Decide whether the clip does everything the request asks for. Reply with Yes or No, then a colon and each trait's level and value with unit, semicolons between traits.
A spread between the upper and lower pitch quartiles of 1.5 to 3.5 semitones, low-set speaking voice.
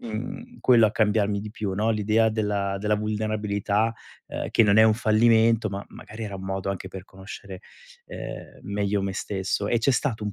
Yes: narrow, 1.9 semitones; low, 105 Hz